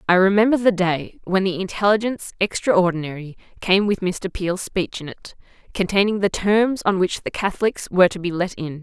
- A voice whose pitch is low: No, high, 190 Hz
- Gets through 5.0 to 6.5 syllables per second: Yes, 5.3 syllables/s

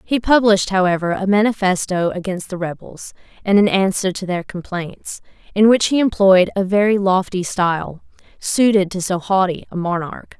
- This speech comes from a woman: Yes, female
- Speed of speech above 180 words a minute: No, average, 160 wpm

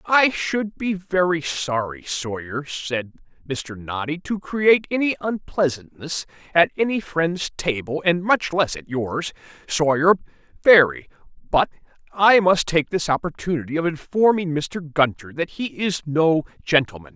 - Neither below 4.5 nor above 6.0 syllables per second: No, 4.2 syllables/s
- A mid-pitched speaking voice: Yes, medium, 165 Hz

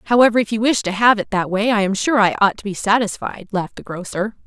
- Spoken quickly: Yes, fast, 270 wpm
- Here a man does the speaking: No, female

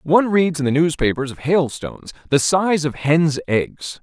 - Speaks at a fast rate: No, average, 180 wpm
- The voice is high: No, medium, 150 Hz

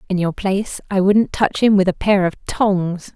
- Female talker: Yes, female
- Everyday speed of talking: No, fast, 230 wpm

